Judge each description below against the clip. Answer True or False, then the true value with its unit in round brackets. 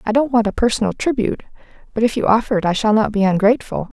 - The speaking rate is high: True (240 wpm)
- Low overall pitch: False (220 Hz)